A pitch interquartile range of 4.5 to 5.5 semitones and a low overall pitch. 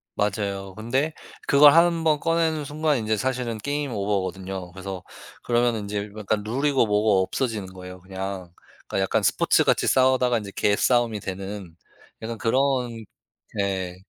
Yes: average, 5.1 semitones; low, 110 Hz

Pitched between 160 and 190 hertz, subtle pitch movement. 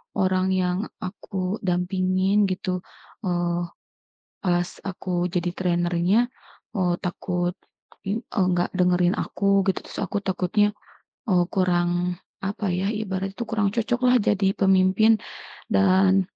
Yes: medium, 185 Hz; narrow, 1.8 semitones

